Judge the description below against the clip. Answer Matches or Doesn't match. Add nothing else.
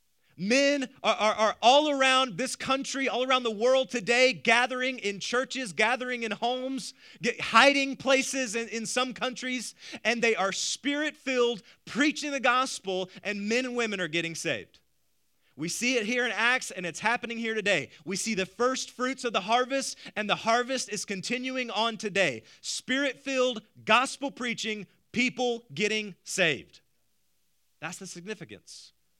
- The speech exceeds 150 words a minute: Matches